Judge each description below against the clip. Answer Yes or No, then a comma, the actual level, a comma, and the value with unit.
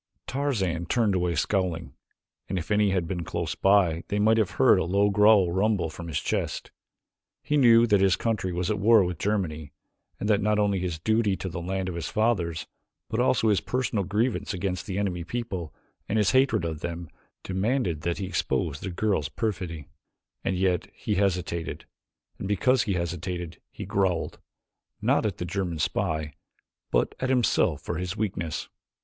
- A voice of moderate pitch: No, very low, 95 Hz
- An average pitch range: Yes, average, 3.7 semitones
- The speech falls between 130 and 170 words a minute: No, average, 180 wpm